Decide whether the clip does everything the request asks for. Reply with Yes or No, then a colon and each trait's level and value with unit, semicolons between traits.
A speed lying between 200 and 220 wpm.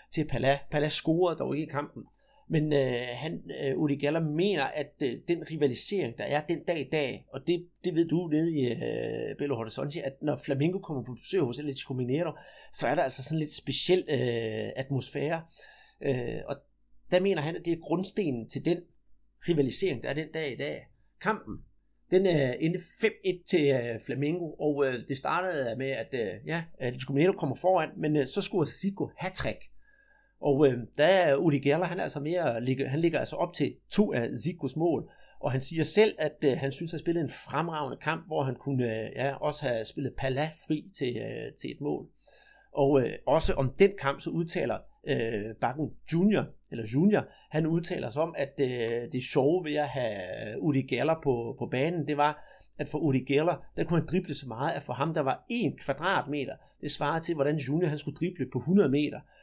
Yes: average, 205 wpm